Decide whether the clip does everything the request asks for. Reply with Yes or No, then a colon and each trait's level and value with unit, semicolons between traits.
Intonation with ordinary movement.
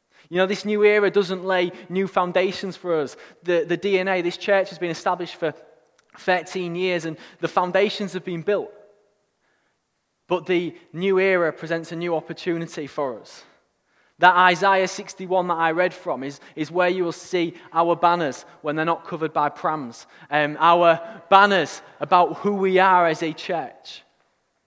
No: narrow, 2.3 semitones